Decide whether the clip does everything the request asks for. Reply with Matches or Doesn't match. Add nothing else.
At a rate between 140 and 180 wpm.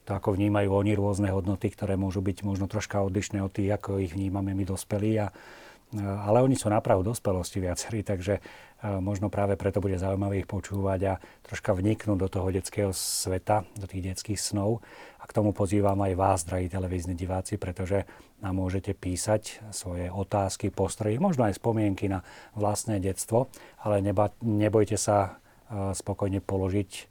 Matches